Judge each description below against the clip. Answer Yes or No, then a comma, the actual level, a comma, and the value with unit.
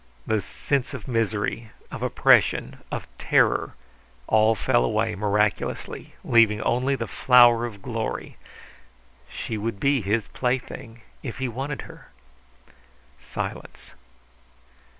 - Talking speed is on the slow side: Yes, slow, 110 wpm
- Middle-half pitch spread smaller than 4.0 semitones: Yes, average, 2.7 semitones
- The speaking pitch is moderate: No, low, 115 Hz